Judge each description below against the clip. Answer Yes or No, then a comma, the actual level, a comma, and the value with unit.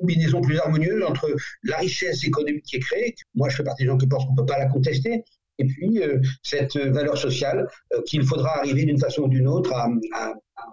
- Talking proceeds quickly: Yes, fast, 235 wpm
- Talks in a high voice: No, medium, 140 Hz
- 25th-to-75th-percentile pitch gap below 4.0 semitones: Yes, narrow, 2.5 semitones